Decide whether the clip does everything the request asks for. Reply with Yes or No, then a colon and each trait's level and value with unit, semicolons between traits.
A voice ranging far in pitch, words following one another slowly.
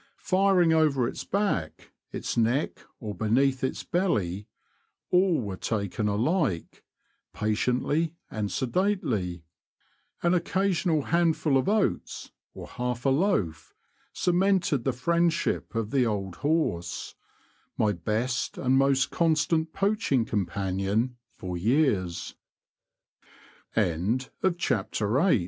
Yes: wide, 7.8 semitones; slow, 95 wpm